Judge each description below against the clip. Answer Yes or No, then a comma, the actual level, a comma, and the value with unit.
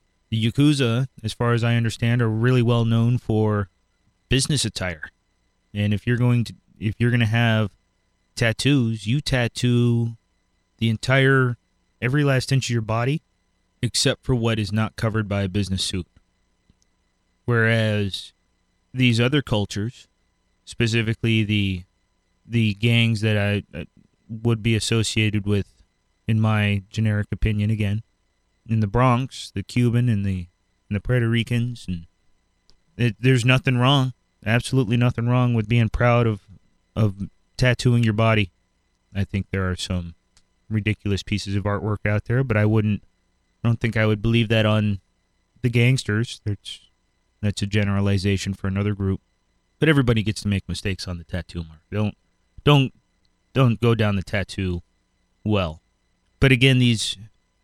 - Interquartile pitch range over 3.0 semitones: Yes, average, 3.5 semitones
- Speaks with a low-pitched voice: Yes, low, 110 Hz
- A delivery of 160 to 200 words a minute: No, average, 150 wpm